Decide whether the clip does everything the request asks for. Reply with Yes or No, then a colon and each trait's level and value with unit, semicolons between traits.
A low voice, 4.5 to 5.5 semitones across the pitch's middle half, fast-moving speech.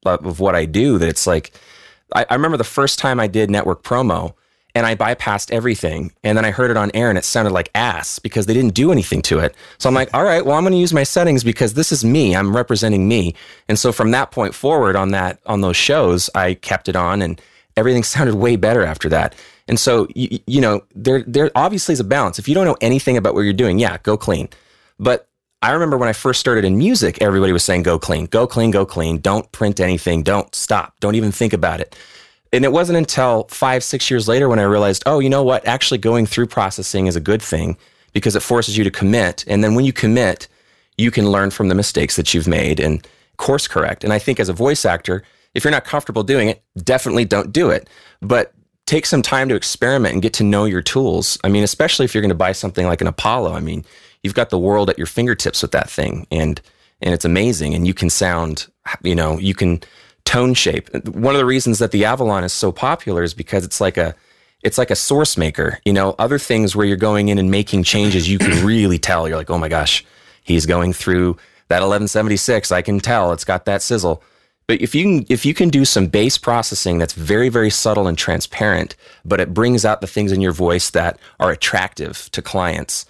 Yes: low, 105 Hz; average, 4.9 semitones; fast, 235 wpm